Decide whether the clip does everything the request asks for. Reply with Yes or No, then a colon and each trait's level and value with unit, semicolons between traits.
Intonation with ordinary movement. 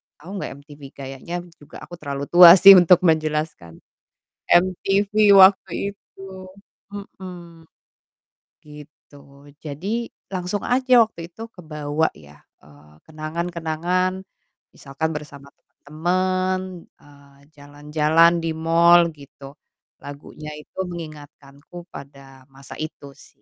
Yes: average, 3.7 semitones